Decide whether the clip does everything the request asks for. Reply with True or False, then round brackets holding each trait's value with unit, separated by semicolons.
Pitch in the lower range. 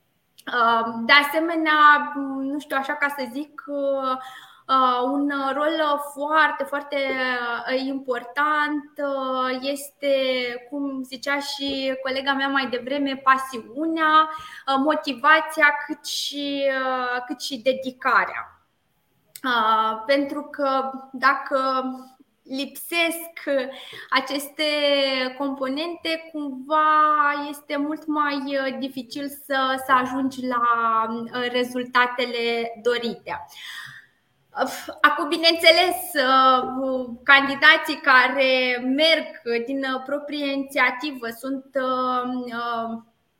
False (275 Hz)